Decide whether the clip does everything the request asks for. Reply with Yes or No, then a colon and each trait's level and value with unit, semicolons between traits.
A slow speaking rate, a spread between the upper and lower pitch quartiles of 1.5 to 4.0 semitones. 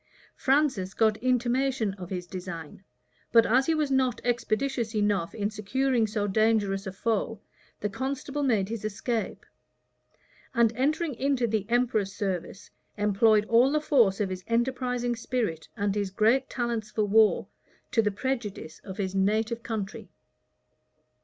No: average, 145 wpm; average, 3.7 semitones